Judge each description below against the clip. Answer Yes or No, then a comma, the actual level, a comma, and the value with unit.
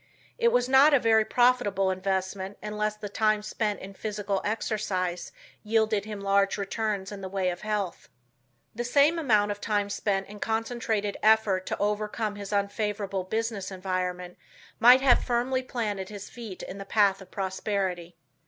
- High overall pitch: Yes, high, 205 Hz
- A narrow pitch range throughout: Yes, narrow, 2.3 semitones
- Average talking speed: Yes, average, 160 wpm